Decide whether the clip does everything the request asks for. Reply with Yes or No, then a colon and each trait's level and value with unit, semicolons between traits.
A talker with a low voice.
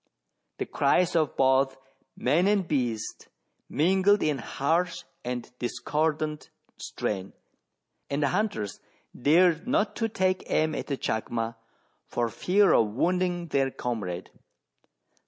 No: medium, 150 Hz